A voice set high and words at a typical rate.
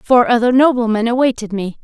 Yes: high, 235 Hz; average, 165 wpm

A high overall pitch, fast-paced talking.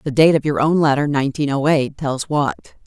No: medium, 145 Hz; fast, 230 wpm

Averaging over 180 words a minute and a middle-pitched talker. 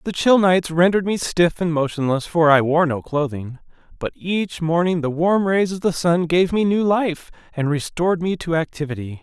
Yes: average, 200 wpm; medium, 170 Hz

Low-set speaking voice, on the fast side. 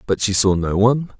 Yes: low, 105 Hz; fast, 250 wpm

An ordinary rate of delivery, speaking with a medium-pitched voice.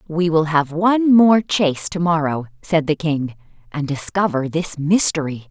Yes: average, 165 wpm; medium, 160 Hz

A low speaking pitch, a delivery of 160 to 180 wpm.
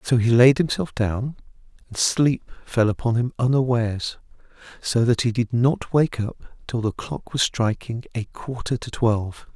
Yes: low, 120 Hz; average, 170 wpm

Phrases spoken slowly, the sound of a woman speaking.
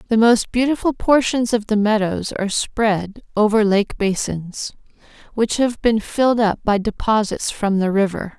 No: average, 155 wpm; female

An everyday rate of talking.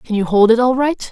No: fast, 325 wpm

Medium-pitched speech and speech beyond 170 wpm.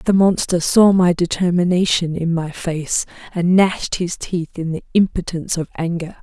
No: medium, 175 Hz; average, 165 wpm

